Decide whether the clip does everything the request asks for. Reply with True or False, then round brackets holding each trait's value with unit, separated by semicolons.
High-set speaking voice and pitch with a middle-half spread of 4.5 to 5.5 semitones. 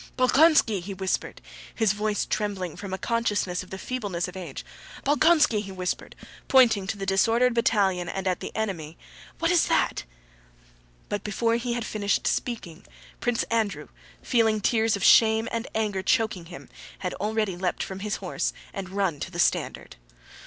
False (205 Hz; 3.4 semitones)